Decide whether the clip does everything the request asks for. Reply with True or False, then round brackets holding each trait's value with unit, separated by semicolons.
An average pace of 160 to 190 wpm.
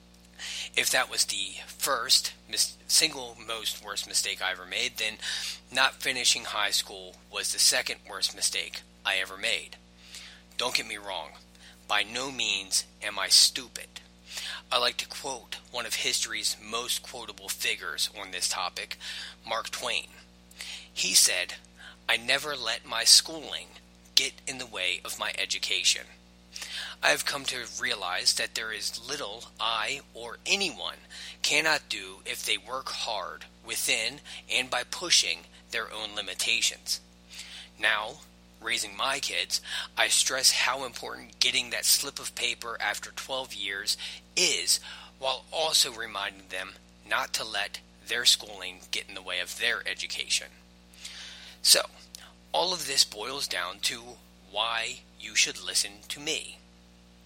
False (145 wpm)